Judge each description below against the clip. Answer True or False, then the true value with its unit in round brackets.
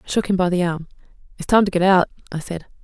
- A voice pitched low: False (180 Hz)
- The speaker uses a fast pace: True (275 wpm)